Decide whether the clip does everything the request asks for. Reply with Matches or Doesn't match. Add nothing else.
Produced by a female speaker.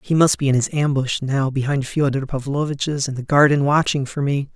Doesn't match